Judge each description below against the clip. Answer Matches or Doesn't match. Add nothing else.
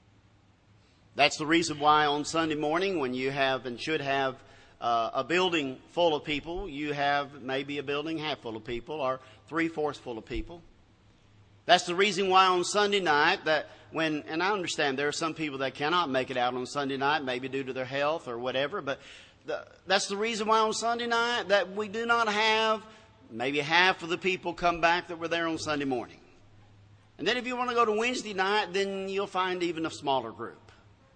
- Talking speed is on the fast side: Matches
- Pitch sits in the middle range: Matches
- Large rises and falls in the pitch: Matches